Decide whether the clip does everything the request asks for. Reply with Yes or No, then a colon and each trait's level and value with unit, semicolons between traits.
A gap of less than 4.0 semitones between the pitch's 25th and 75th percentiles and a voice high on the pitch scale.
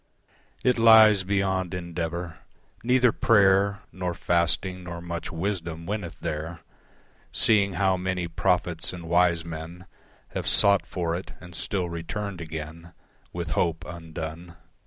No: narrow, 2.5 semitones; very low, 90 Hz